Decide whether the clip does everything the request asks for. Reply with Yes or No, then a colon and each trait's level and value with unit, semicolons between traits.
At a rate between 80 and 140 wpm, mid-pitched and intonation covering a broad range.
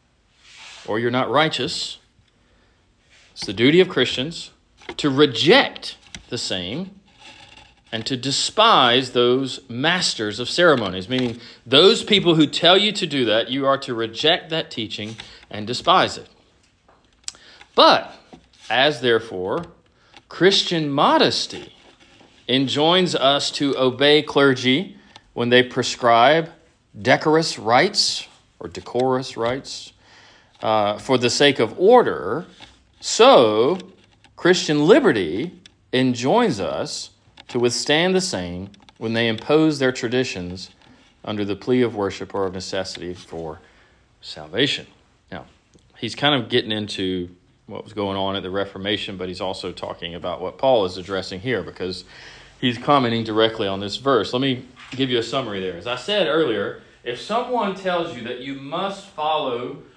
No: slow, 135 wpm; low, 125 Hz; wide, 5.9 semitones